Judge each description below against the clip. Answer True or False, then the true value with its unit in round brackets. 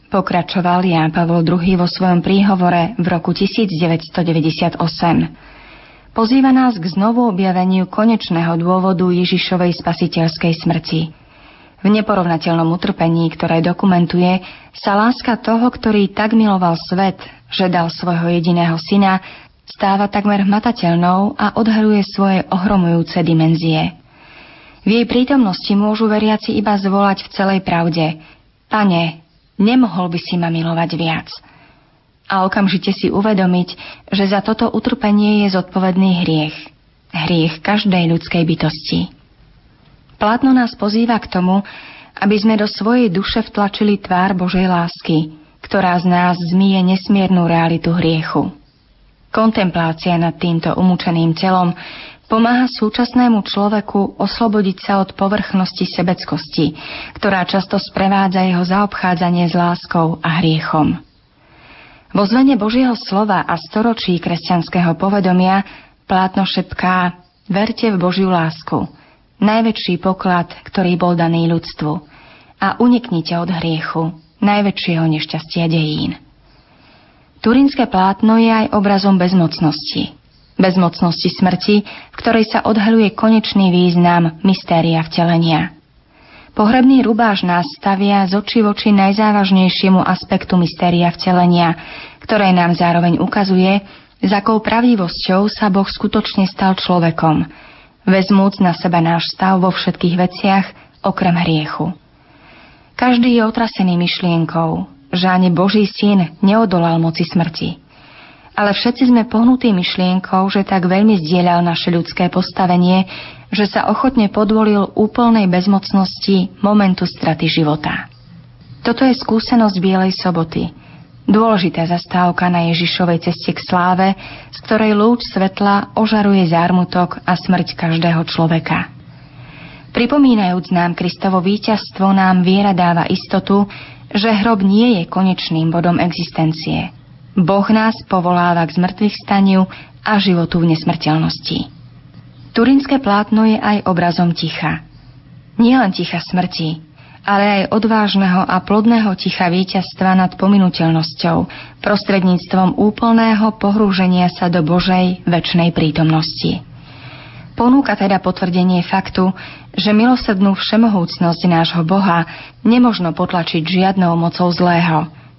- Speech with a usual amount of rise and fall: True (3.2 semitones)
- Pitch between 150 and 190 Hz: True (185 Hz)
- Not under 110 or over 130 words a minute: True (115 wpm)